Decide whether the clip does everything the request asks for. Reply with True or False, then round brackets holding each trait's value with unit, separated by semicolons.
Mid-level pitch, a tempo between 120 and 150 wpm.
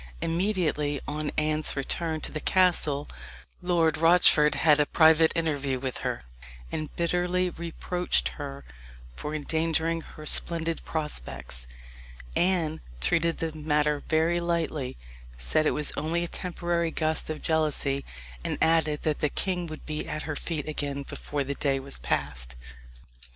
True (155 Hz; 140 wpm)